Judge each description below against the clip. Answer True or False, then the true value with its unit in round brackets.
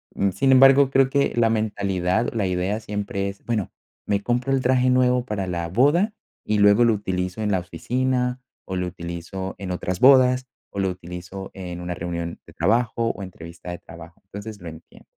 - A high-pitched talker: False (100 Hz)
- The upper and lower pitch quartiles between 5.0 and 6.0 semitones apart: True (5.5 semitones)